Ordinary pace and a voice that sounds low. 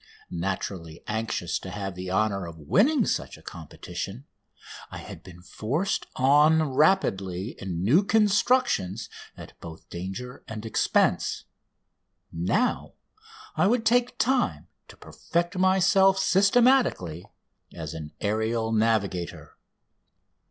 No: slow, 110 wpm; low, 110 Hz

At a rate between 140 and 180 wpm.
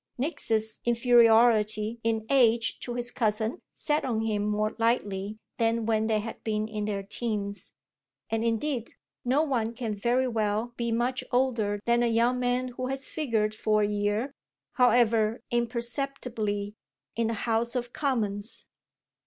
Yes: average, 145 wpm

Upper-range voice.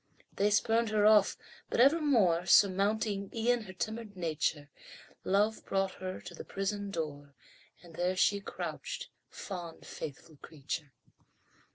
Yes: high, 195 Hz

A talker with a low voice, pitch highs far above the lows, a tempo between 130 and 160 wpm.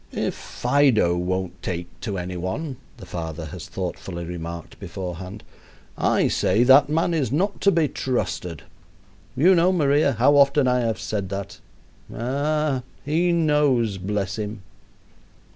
Yes: low, 120 Hz; wide, 7.9 semitones; average, 140 wpm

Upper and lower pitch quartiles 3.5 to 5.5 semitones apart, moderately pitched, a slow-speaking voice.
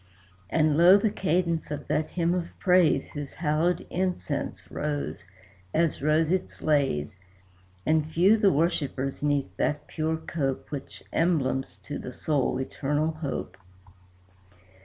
No: average, 2.9 semitones; medium, 155 Hz; slow, 130 wpm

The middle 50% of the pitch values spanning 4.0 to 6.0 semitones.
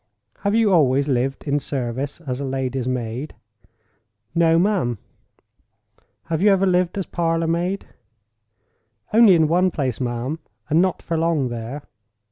Yes: average, 5.3 semitones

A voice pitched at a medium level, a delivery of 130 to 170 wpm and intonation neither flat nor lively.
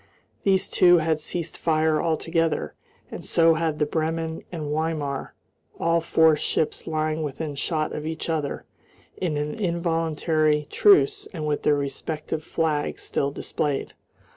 No: medium, 160 Hz; average, 140 wpm; narrow, 1.5 semitones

